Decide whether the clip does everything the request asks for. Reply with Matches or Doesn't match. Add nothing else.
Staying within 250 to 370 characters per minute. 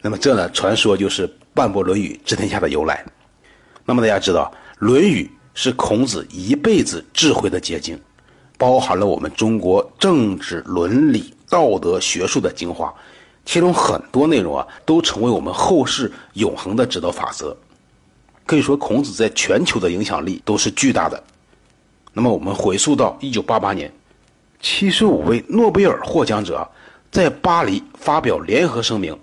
Doesn't match